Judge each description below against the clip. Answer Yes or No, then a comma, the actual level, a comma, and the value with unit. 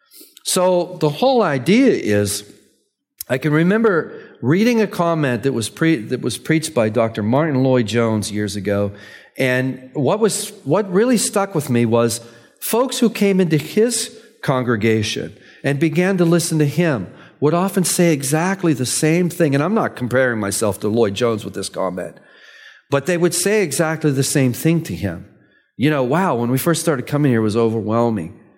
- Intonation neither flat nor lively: No, wide, 7.4 semitones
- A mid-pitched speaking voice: Yes, medium, 150 Hz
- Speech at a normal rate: Yes, average, 180 wpm